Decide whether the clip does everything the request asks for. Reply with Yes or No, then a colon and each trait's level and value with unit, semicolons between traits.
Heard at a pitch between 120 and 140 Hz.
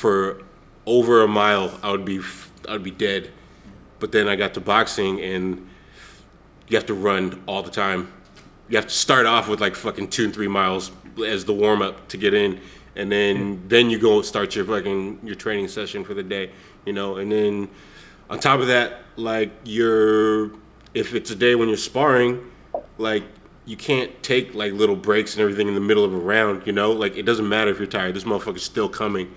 No: low, 105 Hz